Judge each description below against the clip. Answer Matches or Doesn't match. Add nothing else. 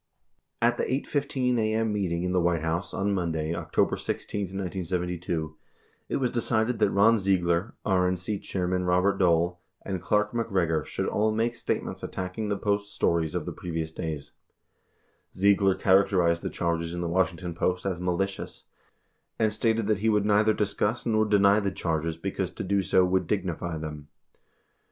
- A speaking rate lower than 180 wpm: Matches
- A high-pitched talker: Doesn't match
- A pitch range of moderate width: Matches